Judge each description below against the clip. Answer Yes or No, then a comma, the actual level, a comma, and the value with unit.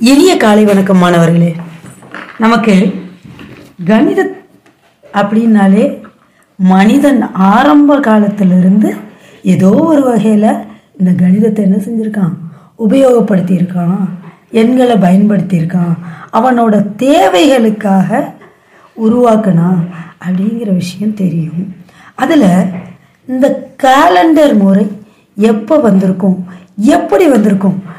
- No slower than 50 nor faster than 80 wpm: Yes, slow, 75 wpm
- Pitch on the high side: Yes, high, 200 Hz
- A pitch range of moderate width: Yes, average, 4.3 semitones